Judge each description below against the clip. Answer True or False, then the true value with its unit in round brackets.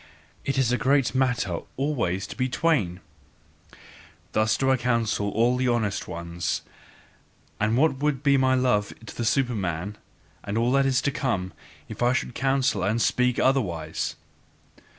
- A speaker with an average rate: True (155 wpm)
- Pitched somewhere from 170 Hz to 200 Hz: False (125 Hz)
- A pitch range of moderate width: True (4.4 semitones)